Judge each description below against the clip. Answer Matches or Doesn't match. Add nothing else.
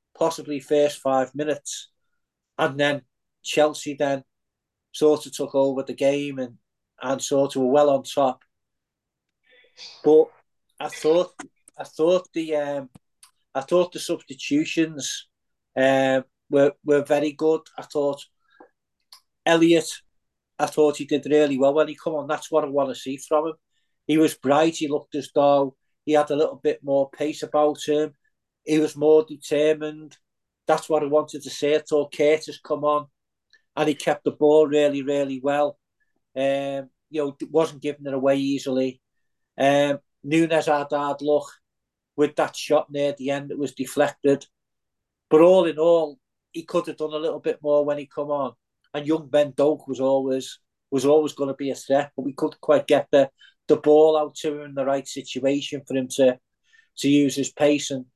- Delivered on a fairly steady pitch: Matches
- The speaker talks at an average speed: Matches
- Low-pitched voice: Doesn't match